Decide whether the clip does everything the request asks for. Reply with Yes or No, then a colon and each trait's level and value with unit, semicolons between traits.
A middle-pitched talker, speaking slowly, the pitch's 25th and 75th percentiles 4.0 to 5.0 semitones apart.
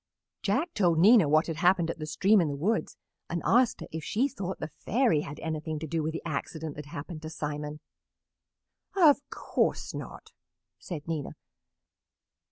No: medium, 165 Hz; average, 175 wpm; average, 4.4 semitones